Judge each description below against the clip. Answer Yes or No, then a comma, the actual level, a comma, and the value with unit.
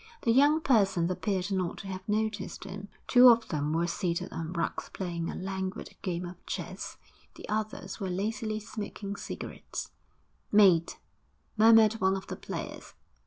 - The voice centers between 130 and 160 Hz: No, high, 195 Hz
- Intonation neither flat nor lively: Yes, average, 3.2 semitones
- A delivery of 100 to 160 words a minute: Yes, average, 155 wpm